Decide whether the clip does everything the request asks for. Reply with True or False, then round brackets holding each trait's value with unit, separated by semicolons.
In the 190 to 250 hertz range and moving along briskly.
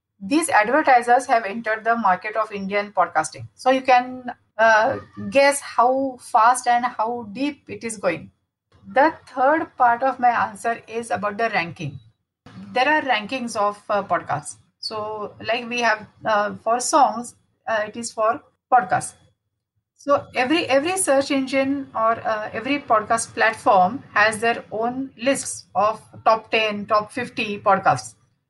True (230 Hz; 145 wpm)